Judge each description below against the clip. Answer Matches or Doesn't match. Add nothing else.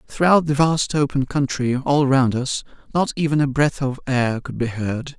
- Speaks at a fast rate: Doesn't match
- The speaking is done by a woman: Doesn't match